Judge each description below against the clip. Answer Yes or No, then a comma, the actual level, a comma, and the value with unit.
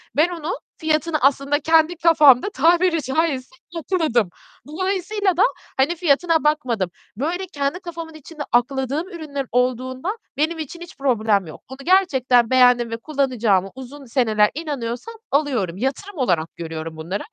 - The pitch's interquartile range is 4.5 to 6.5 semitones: Yes, average, 5.1 semitones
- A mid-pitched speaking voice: No, very high, 280 Hz